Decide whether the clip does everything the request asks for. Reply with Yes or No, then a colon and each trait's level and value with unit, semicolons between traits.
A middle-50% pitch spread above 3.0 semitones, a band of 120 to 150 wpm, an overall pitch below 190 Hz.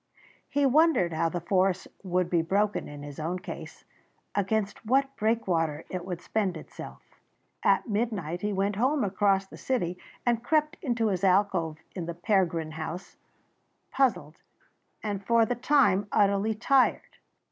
No: average, 4.7 semitones; average, 145 wpm; high, 195 Hz